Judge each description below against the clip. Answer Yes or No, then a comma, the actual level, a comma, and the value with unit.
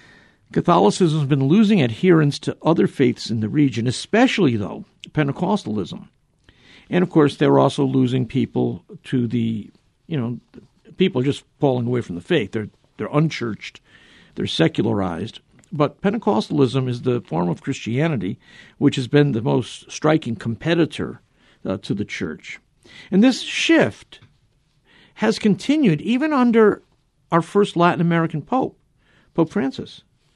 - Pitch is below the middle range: No, medium, 150 Hz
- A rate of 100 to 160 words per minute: Yes, slow, 135 wpm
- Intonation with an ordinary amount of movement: No, wide, 7.0 semitones